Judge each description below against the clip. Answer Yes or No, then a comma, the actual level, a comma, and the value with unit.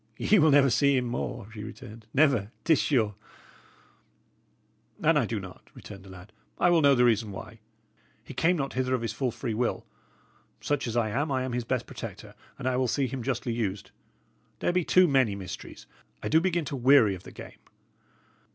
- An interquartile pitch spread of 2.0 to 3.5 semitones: No, average, 4.2 semitones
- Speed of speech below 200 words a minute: No, fast, 205 wpm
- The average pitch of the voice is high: No, low, 125 Hz